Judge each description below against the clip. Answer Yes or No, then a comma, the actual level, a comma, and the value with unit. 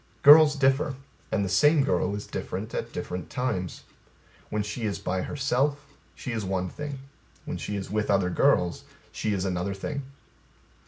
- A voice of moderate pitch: No, low, 105 Hz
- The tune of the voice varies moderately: No, wide, 6.4 semitones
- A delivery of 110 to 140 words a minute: No, average, 165 wpm